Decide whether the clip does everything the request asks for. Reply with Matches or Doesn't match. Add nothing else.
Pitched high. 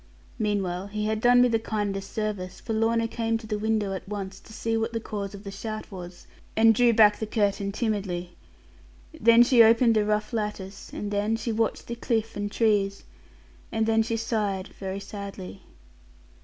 Matches